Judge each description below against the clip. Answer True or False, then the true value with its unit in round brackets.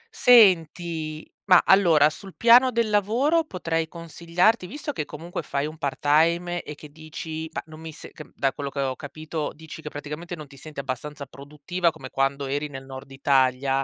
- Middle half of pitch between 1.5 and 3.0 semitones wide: False (3.6 semitones)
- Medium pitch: True (155 Hz)